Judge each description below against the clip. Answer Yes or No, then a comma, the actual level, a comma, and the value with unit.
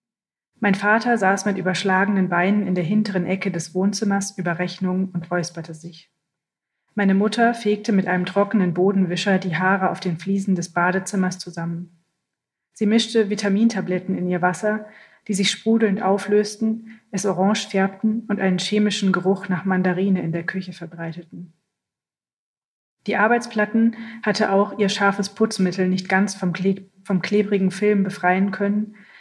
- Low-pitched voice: No, high, 195 Hz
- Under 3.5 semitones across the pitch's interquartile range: Yes, narrow, 2.4 semitones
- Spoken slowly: No, average, 145 wpm